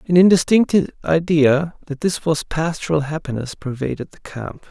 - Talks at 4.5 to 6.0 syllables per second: Yes, 5.0 syllables/s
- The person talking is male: Yes, male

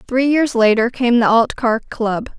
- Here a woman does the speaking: Yes, female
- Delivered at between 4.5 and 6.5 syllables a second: No, 4.2 syllables/s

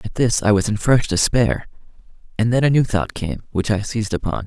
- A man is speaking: Yes, male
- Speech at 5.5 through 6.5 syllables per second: Yes, 5.6 syllables/s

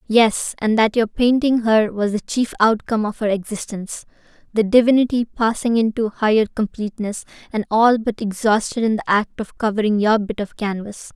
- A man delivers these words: No, female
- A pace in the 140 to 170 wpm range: Yes, average, 165 wpm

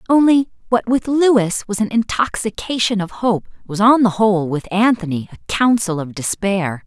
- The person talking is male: No, female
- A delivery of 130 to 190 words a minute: Yes, average, 165 wpm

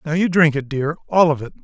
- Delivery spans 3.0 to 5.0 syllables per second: No, 6.1 syllables/s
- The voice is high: No, medium, 155 Hz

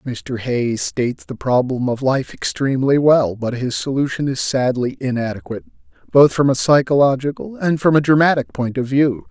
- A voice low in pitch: Yes, low, 130 Hz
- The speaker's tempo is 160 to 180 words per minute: Yes, average, 170 wpm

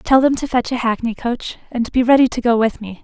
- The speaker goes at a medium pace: No, fast, 275 wpm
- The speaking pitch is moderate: No, high, 240 Hz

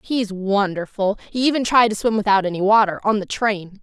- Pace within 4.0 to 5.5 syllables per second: Yes, 5.2 syllables/s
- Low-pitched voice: No, high, 205 Hz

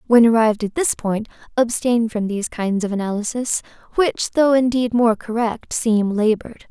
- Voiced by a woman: Yes, female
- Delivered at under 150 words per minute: No, average, 160 wpm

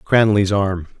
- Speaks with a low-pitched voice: Yes, low, 100 Hz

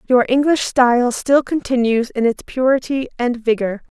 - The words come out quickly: No, average, 150 wpm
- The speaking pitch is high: Yes, very high, 250 Hz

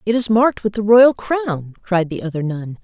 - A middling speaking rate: No, fast, 235 wpm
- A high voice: Yes, high, 195 Hz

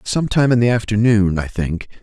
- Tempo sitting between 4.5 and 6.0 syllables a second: Yes, 5.0 syllables/s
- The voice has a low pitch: Yes, low, 110 Hz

